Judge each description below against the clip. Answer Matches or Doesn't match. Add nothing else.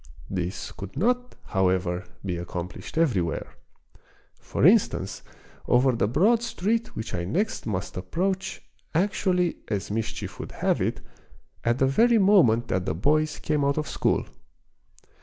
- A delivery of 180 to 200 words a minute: Doesn't match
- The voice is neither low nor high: Doesn't match